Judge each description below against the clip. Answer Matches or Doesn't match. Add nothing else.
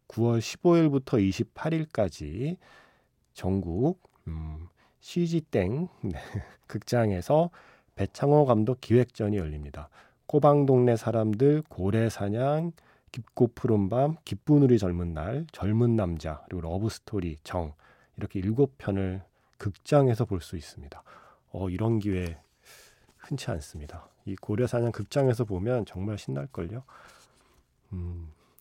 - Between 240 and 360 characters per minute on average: Doesn't match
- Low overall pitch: Matches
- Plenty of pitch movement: Matches